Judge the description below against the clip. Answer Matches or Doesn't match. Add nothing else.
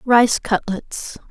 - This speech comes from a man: Doesn't match